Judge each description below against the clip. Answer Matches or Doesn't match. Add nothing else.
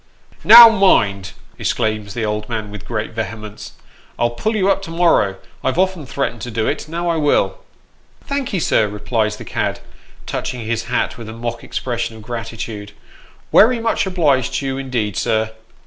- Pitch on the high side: Doesn't match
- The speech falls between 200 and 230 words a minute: Doesn't match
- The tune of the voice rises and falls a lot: Matches